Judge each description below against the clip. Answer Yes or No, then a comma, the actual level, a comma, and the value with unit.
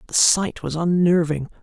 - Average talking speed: Yes, average, 150 wpm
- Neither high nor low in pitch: Yes, medium, 170 Hz